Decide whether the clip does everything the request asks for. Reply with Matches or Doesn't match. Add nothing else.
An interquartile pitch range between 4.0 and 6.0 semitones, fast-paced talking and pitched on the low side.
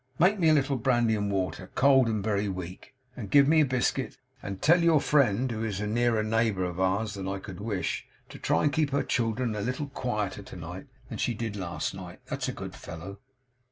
Matches